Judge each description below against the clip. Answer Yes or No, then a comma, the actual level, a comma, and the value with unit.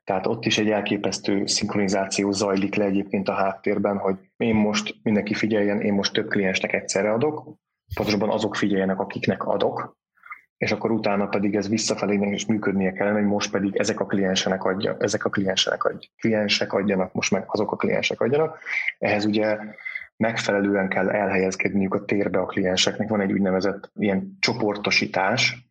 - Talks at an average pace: No, fast, 165 wpm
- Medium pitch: No, low, 100 Hz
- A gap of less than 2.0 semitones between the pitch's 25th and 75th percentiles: Yes, narrow, 1.4 semitones